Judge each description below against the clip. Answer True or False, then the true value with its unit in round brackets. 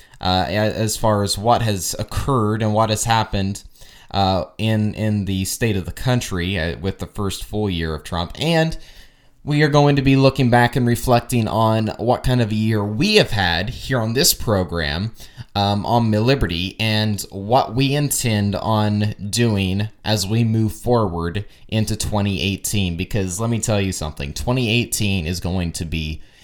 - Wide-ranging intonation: False (3.7 semitones)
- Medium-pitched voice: False (105 Hz)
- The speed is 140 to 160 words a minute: False (170 wpm)